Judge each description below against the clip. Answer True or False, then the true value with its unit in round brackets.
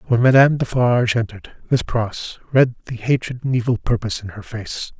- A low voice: True (120 Hz)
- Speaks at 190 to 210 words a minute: False (180 wpm)